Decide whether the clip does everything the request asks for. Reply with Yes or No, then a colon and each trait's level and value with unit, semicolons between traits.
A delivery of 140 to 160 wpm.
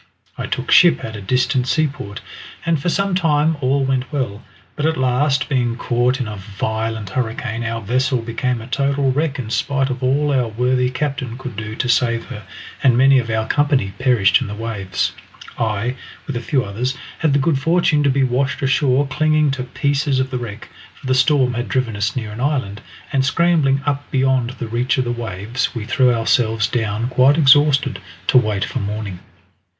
No: average, 195 wpm